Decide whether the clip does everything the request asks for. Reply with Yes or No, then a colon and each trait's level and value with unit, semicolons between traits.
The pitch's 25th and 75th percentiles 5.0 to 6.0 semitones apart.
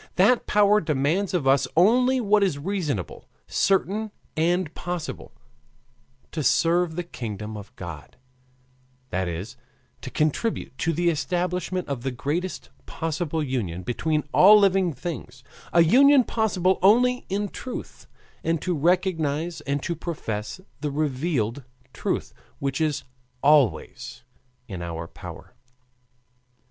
Yes: wide, 5.6 semitones